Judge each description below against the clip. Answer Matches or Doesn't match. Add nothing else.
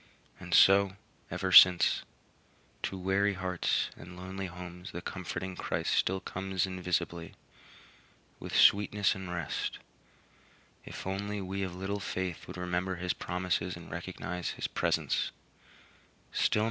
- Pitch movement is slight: Matches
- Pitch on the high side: Doesn't match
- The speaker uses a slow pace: Matches